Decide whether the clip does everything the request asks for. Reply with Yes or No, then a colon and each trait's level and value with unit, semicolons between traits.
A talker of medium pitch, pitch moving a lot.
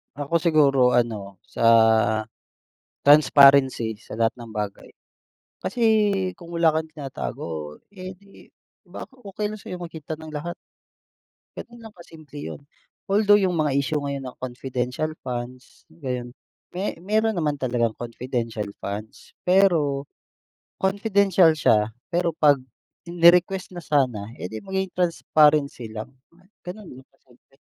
Yes: medium, 150 Hz; wide, 6.4 semitones